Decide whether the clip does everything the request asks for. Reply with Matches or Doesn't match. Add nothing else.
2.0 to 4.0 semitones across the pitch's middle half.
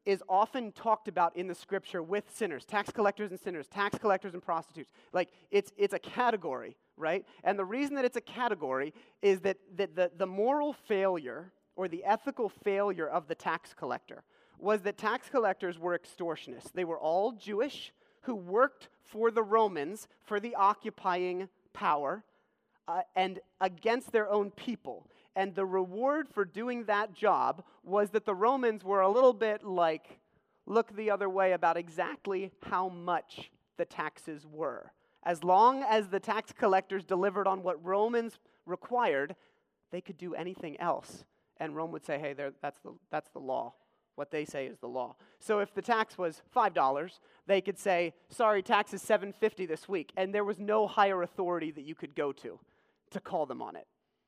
Matches